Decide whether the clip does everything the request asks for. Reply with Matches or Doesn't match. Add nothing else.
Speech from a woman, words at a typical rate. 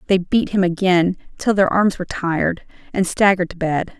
Matches